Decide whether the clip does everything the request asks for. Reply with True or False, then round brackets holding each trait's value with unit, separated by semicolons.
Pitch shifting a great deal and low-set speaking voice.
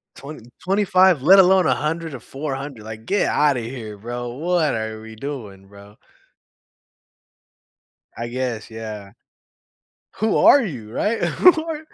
True (8.1 semitones; 130 Hz)